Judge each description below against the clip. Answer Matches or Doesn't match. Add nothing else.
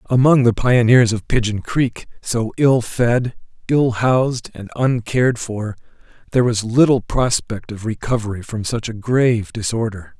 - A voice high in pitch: Doesn't match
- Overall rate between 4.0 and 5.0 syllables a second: Matches